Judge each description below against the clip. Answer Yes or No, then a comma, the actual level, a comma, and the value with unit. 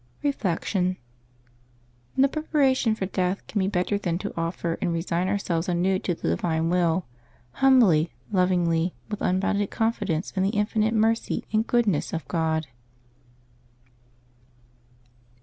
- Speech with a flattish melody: No, average, 4.0 semitones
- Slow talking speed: Yes, slow, 130 wpm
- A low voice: No, medium, 185 Hz